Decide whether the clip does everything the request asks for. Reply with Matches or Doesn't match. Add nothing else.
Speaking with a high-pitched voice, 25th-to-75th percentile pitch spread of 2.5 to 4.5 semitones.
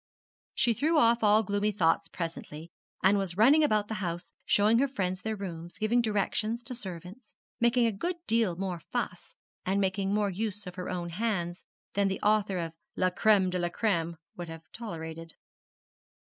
Matches